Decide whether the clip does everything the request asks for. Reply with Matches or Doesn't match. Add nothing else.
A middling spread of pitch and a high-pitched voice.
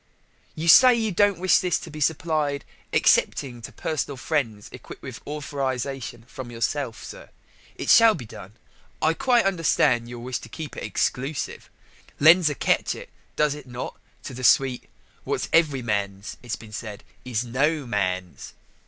Doesn't match